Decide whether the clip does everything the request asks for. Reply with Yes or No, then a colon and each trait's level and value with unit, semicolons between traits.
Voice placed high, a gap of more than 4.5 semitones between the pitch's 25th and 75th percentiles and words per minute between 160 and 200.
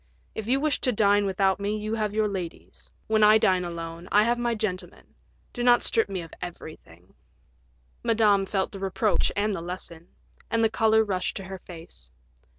No: high, 200 Hz; average, 3.2 semitones; average, 185 wpm